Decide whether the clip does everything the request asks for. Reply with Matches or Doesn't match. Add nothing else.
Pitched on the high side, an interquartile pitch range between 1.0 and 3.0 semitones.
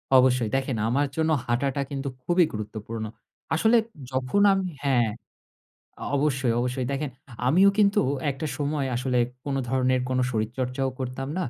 Doesn't match